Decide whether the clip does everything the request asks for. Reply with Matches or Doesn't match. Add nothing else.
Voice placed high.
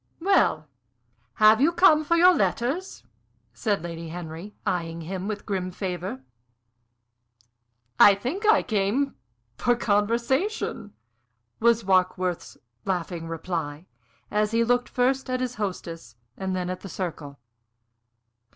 Matches